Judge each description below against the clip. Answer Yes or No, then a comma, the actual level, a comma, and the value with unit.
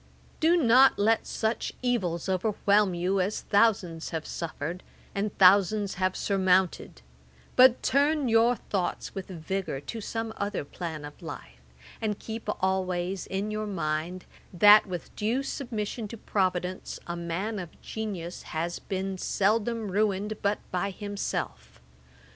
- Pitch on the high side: Yes, high, 195 Hz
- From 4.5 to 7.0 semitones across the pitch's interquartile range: No, average, 3.4 semitones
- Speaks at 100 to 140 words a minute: Yes, slow, 135 wpm